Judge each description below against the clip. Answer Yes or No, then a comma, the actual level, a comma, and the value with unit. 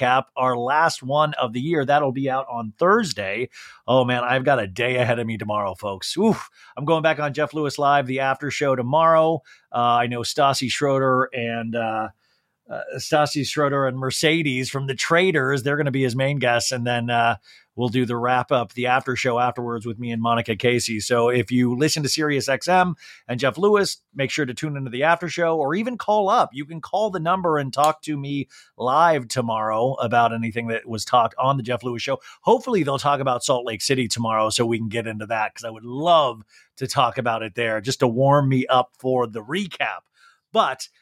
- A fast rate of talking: Yes, fast, 215 wpm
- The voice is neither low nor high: No, low, 130 Hz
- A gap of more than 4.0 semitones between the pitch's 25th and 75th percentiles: No, average, 3.4 semitones